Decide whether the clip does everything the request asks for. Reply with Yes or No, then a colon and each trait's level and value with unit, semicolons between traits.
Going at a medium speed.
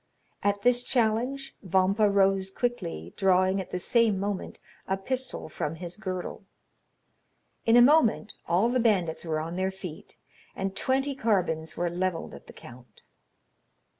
Yes: average, 145 wpm